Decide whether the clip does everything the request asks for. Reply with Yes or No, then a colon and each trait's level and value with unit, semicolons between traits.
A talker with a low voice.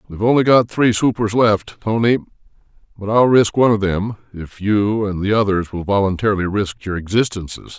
Yes: low, 105 Hz